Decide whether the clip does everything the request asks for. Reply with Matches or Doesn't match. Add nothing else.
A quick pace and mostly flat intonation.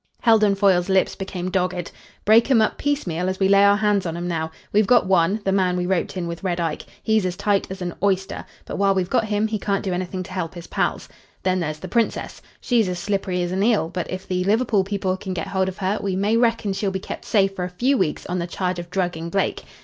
Matches